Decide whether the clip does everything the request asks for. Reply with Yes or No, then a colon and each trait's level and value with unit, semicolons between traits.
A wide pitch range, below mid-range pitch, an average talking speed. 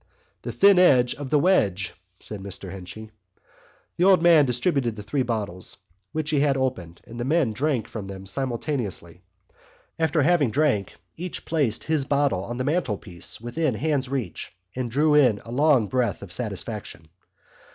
Yes: wide, 6.2 semitones; low, 125 Hz; average, 160 wpm